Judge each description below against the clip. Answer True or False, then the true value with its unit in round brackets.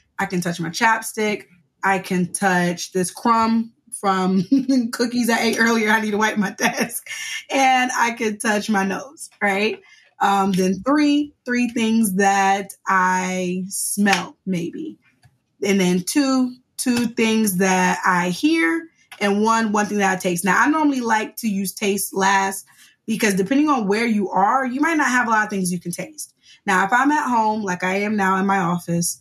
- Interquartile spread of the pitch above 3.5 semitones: True (4.5 semitones)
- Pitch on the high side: True (210 Hz)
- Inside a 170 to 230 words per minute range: True (185 wpm)